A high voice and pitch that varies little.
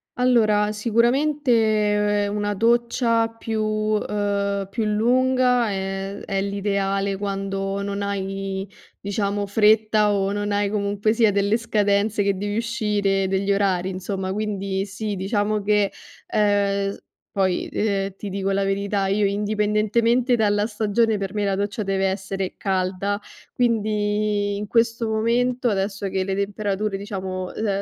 Yes: high, 205 Hz; narrow, 1.5 semitones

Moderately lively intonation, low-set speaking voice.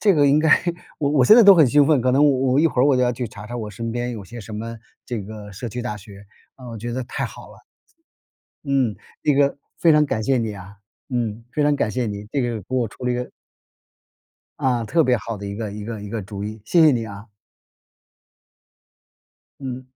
Yes: average, 4.2 semitones; low, 120 Hz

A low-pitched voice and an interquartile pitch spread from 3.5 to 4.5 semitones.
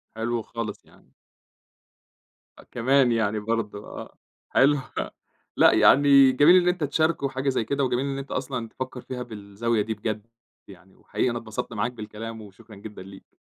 Yes: low, 115 Hz; average, 3.9 semitones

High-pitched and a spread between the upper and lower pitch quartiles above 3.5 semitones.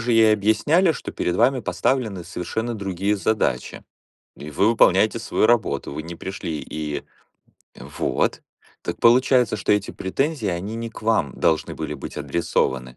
No: low, 105 Hz; average, 5.2 semitones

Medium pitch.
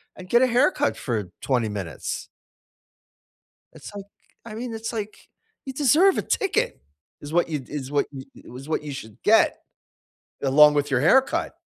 Yes: medium, 150 Hz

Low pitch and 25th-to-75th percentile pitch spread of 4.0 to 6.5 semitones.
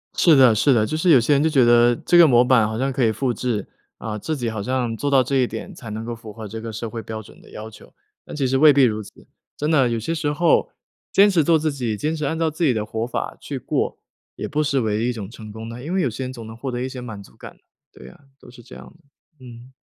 Yes: low, 125 Hz; average, 4.3 semitones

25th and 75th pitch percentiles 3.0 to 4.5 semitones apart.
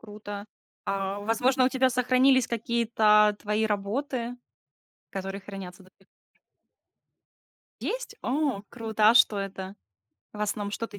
Yes: average, 3.4 semitones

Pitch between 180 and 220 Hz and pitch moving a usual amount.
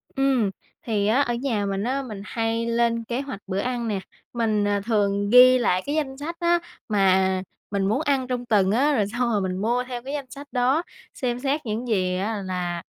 No: high, 230 Hz; average, 4.2 semitones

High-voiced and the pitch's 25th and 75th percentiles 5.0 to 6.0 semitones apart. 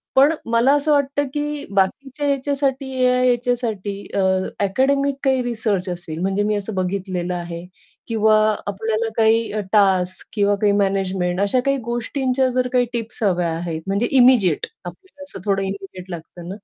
Yes: high, 215 Hz; average, 5.3 semitones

